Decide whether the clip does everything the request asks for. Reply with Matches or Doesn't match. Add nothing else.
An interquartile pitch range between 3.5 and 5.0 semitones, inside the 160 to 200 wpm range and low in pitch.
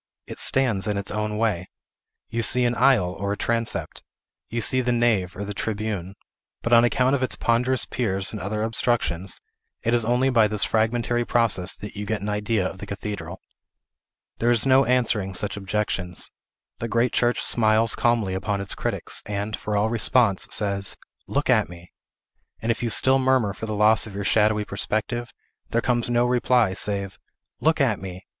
Doesn't match